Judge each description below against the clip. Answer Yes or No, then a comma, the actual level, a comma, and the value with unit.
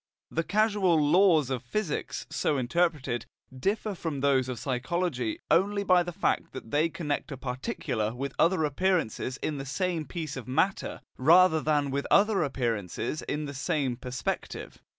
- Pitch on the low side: No, medium, 150 Hz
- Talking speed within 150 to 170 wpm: Yes, average, 155 wpm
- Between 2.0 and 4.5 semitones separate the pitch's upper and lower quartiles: No, wide, 5.5 semitones